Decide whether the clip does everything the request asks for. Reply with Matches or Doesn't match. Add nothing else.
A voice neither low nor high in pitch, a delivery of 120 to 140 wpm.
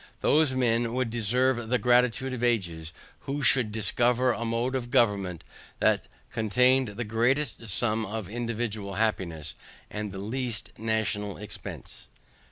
Doesn't match